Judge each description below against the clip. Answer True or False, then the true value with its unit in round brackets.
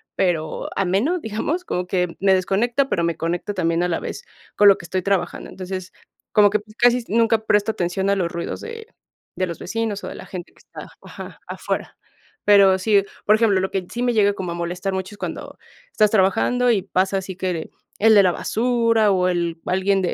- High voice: True (195 Hz)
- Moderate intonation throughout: True (3.3 semitones)